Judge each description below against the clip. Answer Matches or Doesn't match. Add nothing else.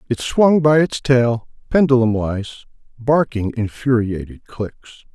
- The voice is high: Doesn't match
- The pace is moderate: Doesn't match